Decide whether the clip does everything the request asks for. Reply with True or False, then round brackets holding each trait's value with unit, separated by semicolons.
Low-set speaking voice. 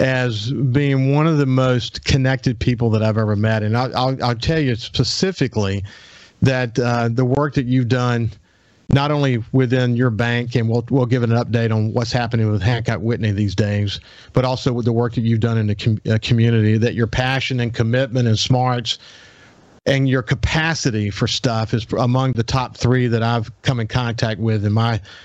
True (120 Hz)